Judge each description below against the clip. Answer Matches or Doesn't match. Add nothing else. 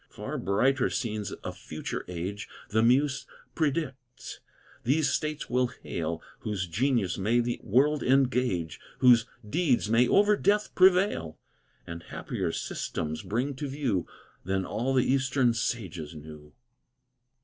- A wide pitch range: Matches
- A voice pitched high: Doesn't match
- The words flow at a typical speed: Doesn't match